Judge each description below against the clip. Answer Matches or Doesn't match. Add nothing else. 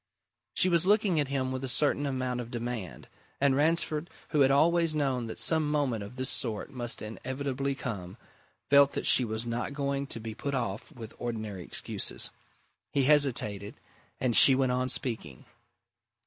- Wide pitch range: Doesn't match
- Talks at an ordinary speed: Matches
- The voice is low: Matches